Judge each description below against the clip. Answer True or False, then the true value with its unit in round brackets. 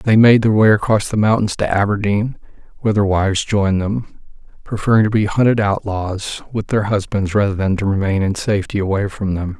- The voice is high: False (105 Hz)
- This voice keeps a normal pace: True (195 wpm)